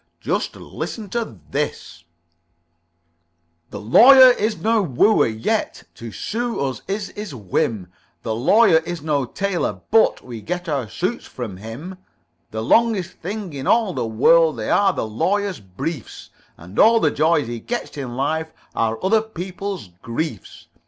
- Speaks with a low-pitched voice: No, medium, 160 Hz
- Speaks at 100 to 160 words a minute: Yes, average, 150 wpm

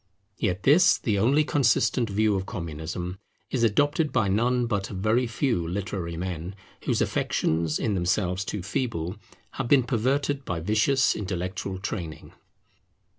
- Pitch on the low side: Yes, low, 100 Hz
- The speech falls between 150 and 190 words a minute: No, average, 140 wpm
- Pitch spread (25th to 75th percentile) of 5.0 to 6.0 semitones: Yes, average, 5.3 semitones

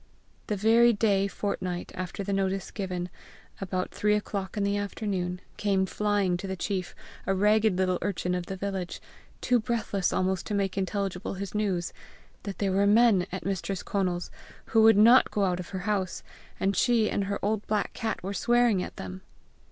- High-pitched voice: Yes, high, 195 Hz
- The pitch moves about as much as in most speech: No, narrow, 2.1 semitones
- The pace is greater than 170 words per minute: Yes, average, 185 wpm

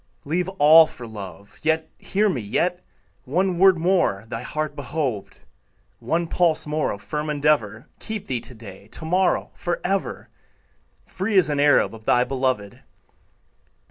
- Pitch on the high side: No, medium, 150 Hz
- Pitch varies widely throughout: Yes, wide, 7.3 semitones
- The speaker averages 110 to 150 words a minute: Yes, average, 145 wpm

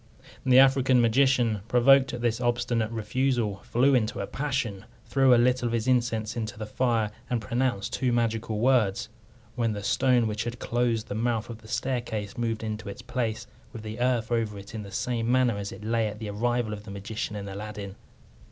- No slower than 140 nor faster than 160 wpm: No, average, 200 wpm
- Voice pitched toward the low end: Yes, low, 115 Hz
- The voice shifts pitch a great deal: No, narrow, 2.4 semitones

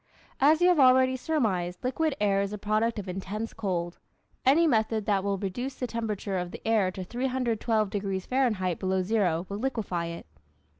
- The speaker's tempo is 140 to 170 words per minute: No, average, 180 wpm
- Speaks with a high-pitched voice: Yes, high, 215 Hz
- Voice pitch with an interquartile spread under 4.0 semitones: No, average, 4.9 semitones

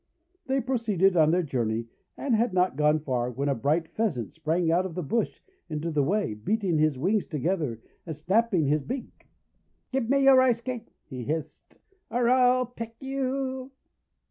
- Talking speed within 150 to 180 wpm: Yes, average, 170 wpm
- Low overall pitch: No, medium, 180 Hz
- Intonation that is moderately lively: No, wide, 8.0 semitones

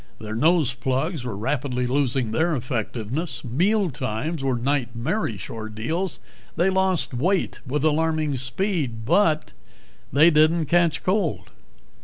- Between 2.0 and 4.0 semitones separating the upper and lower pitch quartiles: No, wide, 5.5 semitones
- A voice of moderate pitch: Yes, medium, 145 Hz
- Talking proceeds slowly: Yes, slow, 115 wpm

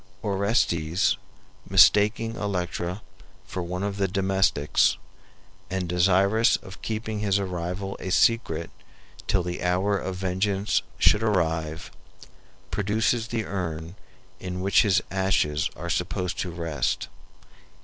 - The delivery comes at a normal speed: No, slow, 115 wpm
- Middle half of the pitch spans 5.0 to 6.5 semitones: No, narrow, 2.6 semitones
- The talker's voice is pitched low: Yes, very low, 95 Hz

